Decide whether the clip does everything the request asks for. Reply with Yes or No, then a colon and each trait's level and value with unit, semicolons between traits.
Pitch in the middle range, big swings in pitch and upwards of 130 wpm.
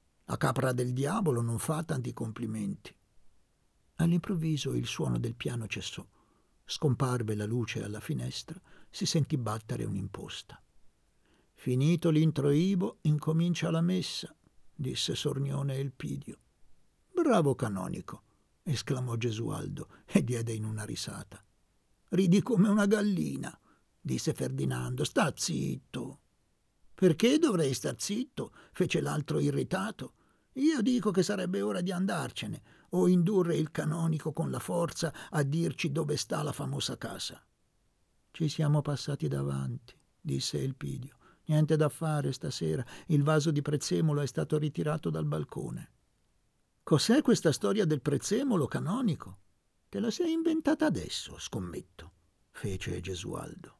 No: medium, 150 Hz; wide, 6.9 semitones; average, 120 wpm